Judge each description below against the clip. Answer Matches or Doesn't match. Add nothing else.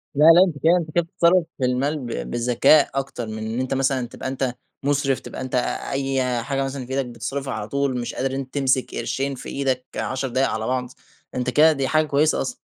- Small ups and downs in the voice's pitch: Matches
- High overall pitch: Doesn't match